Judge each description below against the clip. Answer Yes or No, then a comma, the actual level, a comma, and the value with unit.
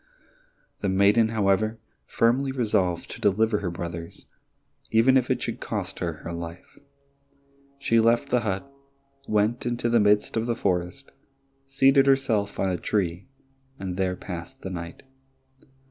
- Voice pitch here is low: Yes, low, 105 Hz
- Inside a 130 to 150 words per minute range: Yes, average, 145 wpm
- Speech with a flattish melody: No, average, 4.3 semitones